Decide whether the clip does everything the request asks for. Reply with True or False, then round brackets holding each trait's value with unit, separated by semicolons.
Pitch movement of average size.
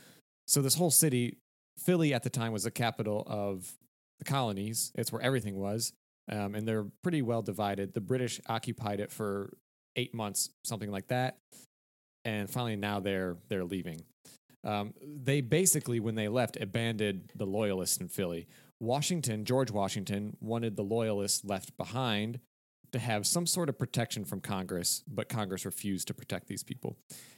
True (3.8 semitones)